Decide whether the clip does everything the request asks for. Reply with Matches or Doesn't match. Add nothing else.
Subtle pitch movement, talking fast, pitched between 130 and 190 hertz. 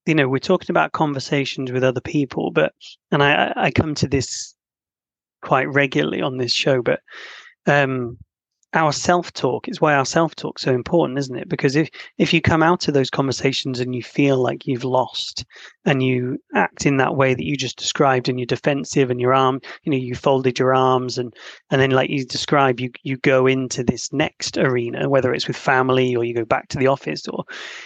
Matches